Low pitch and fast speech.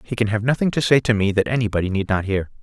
Yes: low, 110 Hz; fast, 295 wpm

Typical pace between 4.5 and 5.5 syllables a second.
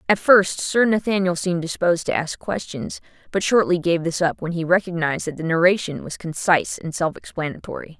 No: 5.7 syllables/s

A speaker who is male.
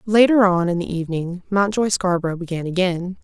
No: female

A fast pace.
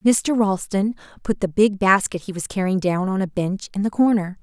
Yes: fast, 215 wpm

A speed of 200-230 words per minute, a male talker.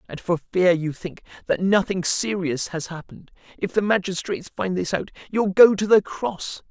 No: average, 190 wpm; male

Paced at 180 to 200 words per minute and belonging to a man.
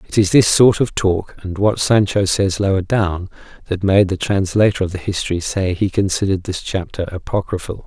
Yes: average, 190 wpm; male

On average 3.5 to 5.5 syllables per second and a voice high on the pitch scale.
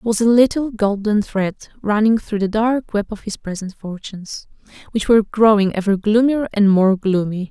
Yes: 5.1 syllables/s; high, 210 Hz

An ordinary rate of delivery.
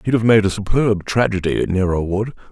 Yes: average, 190 wpm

